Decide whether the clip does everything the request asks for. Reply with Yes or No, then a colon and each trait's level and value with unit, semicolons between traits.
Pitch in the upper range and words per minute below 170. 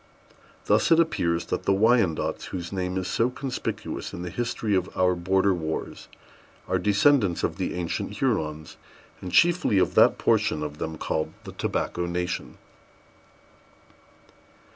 No: very low, 95 Hz; average, 140 wpm